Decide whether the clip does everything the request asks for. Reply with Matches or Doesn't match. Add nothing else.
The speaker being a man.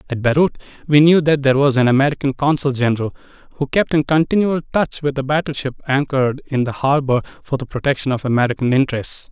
Matches